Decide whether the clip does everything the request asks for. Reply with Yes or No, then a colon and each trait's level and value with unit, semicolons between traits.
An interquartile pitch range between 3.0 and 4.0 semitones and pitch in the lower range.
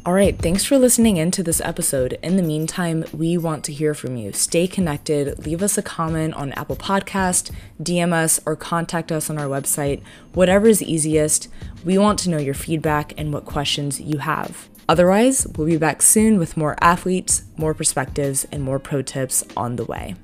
No: average, 3.4 semitones; medium, 160 Hz